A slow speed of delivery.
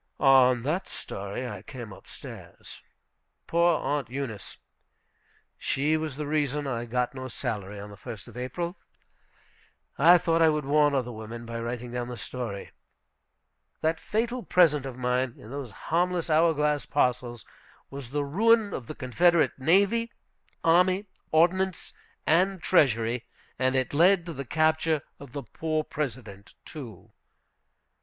No: average, 145 wpm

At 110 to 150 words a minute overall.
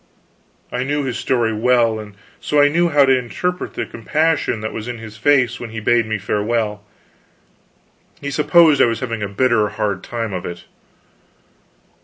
No: average, 175 wpm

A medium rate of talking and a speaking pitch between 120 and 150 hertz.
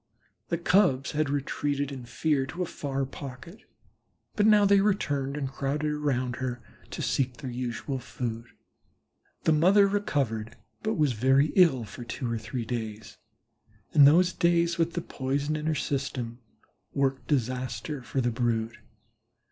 Yes: average, 150 wpm; low, 135 Hz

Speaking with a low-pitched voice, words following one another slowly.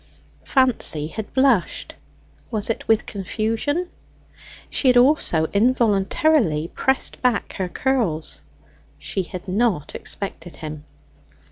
No: high, 215 Hz; slow, 105 wpm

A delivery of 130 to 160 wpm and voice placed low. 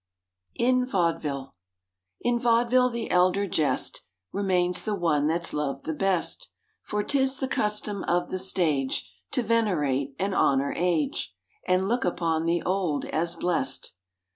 No: average, 140 wpm; medium, 180 Hz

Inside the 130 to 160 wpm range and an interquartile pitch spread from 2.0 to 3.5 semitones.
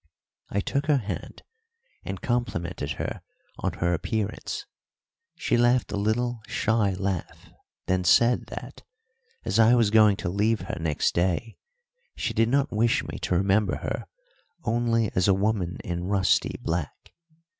No: average, 145 wpm; average, 3.9 semitones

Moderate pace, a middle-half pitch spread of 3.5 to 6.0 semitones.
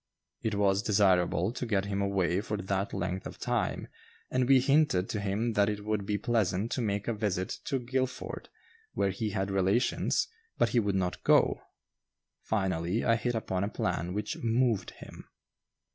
No: average, 175 wpm; average, 3.1 semitones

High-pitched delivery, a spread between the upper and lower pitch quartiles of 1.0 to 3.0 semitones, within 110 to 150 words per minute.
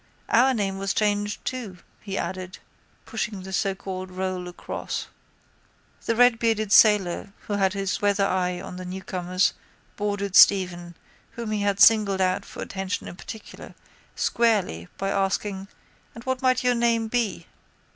Yes: high, 200 Hz; average, 2.7 semitones; average, 145 wpm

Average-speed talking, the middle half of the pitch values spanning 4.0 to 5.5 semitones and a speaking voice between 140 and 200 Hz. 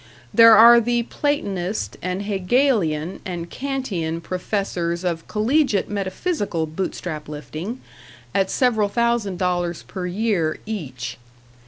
No: slow, 110 wpm; average, 5.2 semitones; high, 190 Hz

